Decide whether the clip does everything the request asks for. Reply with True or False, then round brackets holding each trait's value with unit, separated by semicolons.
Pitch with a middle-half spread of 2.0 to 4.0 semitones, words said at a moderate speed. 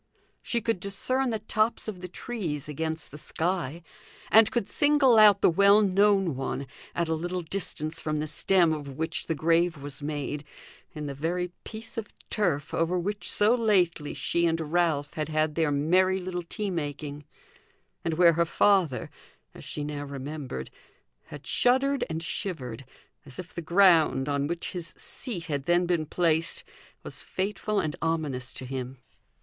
False (4.7 semitones; 165 wpm)